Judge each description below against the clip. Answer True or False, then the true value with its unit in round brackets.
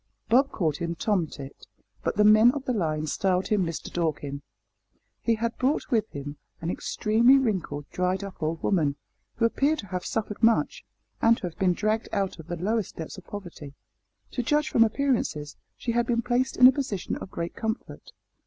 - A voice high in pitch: True (205 Hz)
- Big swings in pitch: True (5.7 semitones)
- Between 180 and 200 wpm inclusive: True (190 wpm)